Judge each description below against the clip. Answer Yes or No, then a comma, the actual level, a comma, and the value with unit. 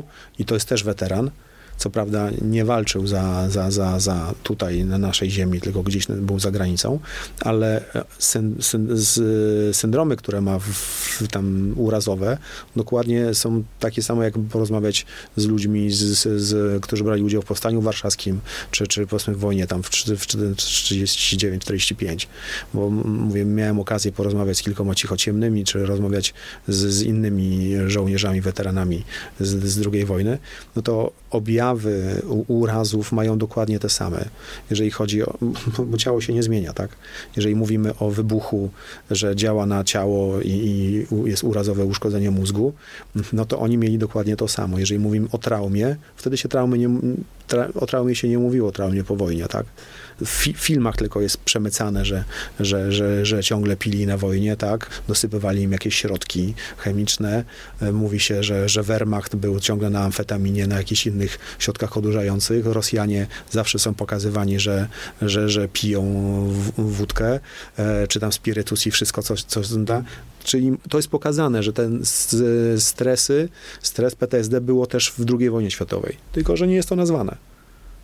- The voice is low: Yes, low, 105 Hz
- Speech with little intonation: Yes, narrow, 2.1 semitones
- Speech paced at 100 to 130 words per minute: No, average, 155 wpm